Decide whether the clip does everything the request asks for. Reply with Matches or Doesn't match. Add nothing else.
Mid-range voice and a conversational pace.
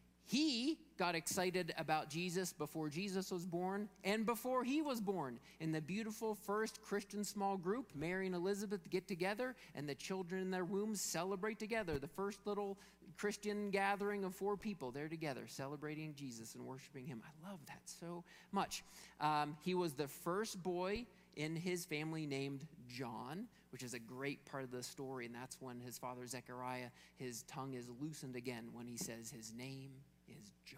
Matches